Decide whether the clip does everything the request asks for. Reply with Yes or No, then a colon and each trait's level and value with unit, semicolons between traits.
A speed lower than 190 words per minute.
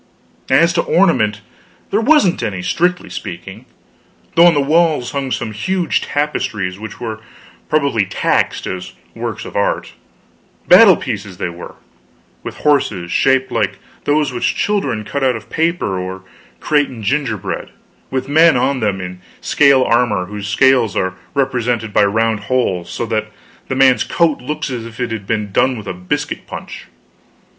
Yes: average, 160 wpm